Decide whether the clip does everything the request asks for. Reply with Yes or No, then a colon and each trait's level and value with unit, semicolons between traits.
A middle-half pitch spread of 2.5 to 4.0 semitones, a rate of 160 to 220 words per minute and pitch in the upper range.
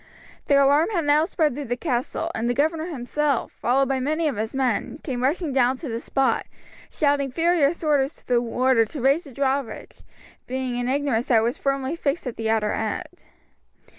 Yes: average, 3.3 semitones; average, 195 wpm; very high, 270 Hz